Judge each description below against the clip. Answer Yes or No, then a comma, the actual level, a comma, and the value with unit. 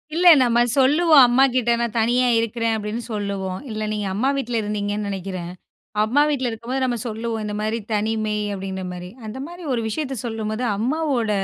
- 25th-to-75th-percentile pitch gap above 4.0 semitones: No, average, 3.2 semitones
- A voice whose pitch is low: No, high, 225 Hz